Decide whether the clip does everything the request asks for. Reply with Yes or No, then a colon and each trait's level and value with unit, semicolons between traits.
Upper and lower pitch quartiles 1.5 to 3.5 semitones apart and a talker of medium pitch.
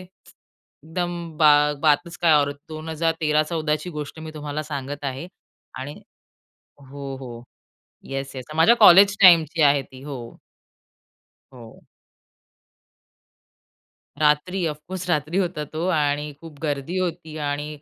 Yes: average, 2.7 semitones; medium, 155 Hz